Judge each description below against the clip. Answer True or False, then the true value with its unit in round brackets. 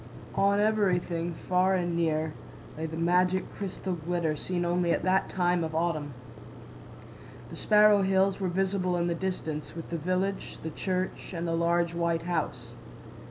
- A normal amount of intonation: False (2.1 semitones)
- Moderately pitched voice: True (175 Hz)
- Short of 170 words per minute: True (150 wpm)